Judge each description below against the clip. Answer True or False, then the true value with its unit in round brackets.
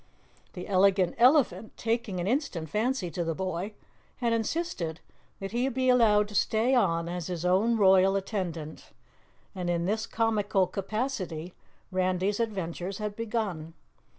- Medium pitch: False (195 Hz)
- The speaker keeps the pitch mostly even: False (4.0 semitones)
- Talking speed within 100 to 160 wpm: True (140 wpm)